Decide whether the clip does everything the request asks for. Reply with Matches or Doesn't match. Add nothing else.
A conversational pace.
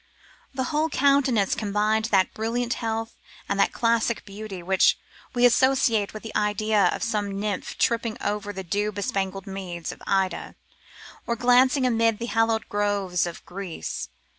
Matches